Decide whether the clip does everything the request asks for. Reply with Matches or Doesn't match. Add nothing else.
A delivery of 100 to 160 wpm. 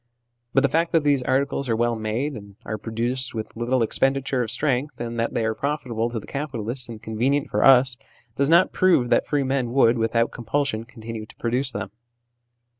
Doesn't match